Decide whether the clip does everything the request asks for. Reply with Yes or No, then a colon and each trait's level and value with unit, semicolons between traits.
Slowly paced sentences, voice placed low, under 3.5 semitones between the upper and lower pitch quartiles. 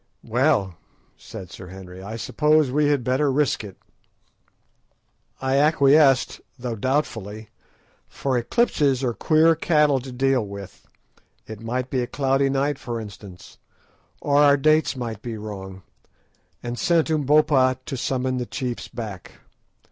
No: slow, 130 wpm; low, 130 Hz; average, 4.5 semitones